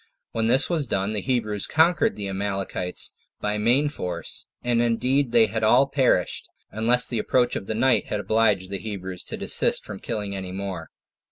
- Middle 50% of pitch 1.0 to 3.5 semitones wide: No, average, 4.0 semitones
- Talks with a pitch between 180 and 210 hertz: No, low, 110 Hz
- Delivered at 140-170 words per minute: No, average, 180 wpm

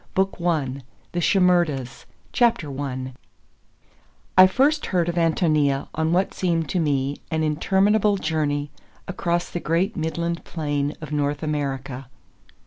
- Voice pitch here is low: No, medium, 160 Hz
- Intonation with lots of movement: No, average, 3.6 semitones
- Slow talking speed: Yes, slow, 125 wpm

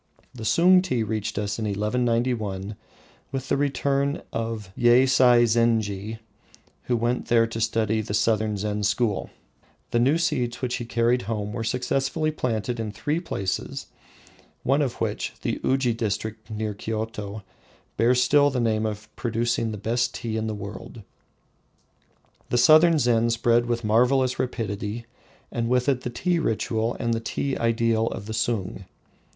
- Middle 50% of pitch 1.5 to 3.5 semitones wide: Yes, narrow, 2.4 semitones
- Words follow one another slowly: No, average, 155 wpm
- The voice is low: Yes, low, 115 Hz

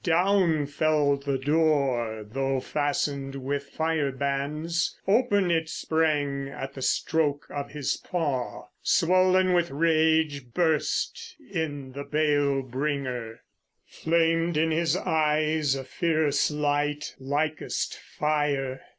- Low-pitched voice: No, medium, 150 Hz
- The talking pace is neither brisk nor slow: No, slow, 110 wpm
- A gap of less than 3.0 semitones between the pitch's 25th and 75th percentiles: Yes, narrow, 2.6 semitones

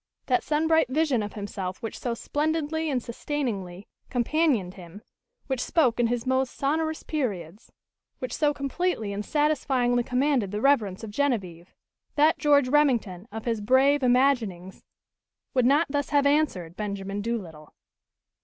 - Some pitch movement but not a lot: No, wide, 6.0 semitones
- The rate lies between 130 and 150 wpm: Yes, average, 145 wpm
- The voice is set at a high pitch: Yes, very high, 250 Hz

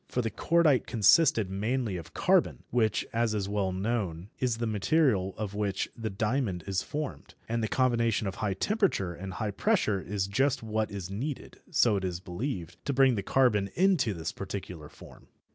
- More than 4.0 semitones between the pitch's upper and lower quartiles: Yes, average, 4.5 semitones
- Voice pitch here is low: Yes, low, 105 Hz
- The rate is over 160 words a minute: Yes, average, 180 wpm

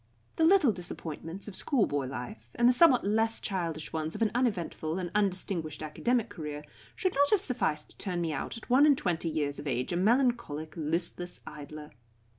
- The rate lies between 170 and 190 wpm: Yes, average, 185 wpm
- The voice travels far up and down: Yes, wide, 7.3 semitones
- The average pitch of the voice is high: No, medium, 180 Hz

